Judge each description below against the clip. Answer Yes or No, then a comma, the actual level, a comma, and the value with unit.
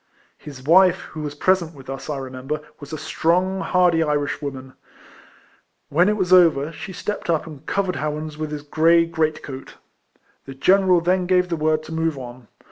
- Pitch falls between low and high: Yes, medium, 155 Hz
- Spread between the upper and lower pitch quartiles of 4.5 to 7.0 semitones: No, average, 3.7 semitones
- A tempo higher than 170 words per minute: Yes, average, 180 wpm